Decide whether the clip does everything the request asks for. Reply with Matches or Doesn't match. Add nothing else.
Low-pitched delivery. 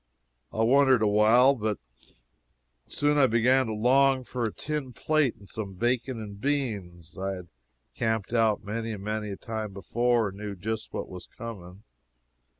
Matches